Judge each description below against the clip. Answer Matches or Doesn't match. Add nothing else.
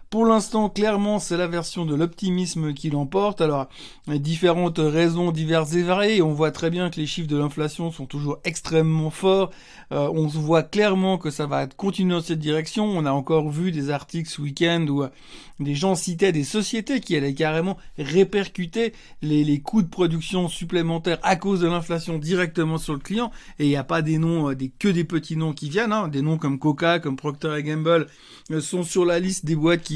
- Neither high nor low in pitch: Matches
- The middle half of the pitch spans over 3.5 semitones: Doesn't match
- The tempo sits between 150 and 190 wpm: Doesn't match